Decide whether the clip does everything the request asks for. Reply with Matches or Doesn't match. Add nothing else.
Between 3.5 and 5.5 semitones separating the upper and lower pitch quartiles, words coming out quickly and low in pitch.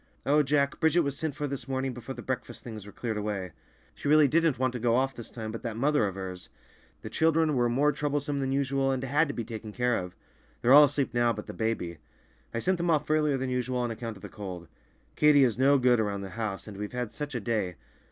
Matches